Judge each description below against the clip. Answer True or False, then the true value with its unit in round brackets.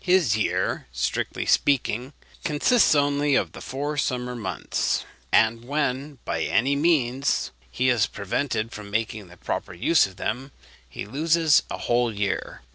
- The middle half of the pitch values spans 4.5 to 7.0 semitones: True (4.8 semitones)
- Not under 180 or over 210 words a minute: False (145 wpm)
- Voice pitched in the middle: False (125 Hz)